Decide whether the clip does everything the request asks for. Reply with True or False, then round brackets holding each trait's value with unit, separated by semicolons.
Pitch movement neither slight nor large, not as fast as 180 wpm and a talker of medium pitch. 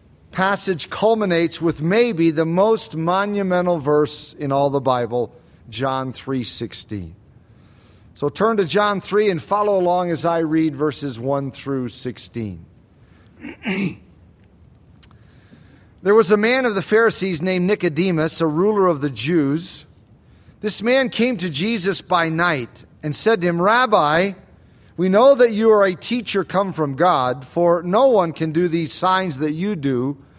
False (6.9 semitones; 150 wpm; 165 Hz)